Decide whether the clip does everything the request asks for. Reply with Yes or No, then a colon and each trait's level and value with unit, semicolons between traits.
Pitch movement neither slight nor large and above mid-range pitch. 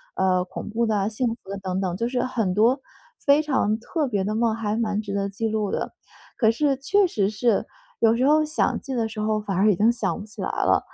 Yes: average, 3.5 semitones; high, 220 Hz